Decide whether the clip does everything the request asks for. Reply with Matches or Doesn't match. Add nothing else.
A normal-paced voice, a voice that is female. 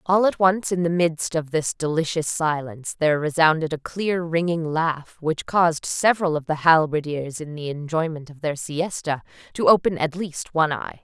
Matches